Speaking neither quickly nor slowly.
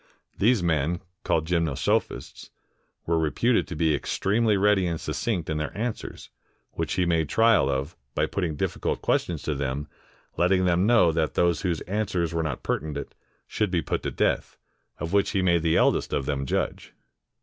Yes: average, 170 wpm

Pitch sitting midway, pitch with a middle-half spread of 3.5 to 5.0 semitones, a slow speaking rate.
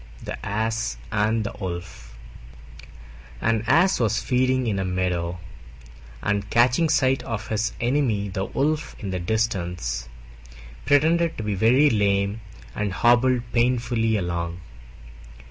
No: low, 110 Hz; average, 4.5 semitones; slow, 125 wpm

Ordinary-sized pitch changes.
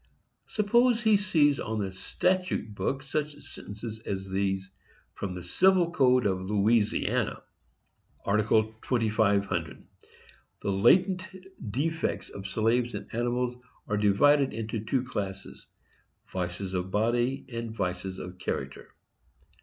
No: wide, 5.9 semitones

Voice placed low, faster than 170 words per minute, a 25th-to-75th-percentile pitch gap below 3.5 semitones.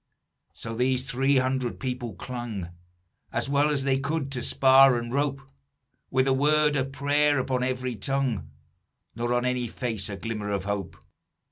No: low, 130 Hz; average, 160 wpm; narrow, 2.5 semitones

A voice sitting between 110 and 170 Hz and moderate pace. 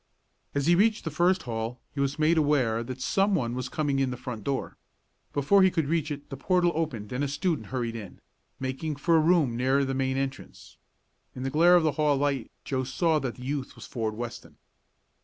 No: medium, 140 Hz; fast, 215 wpm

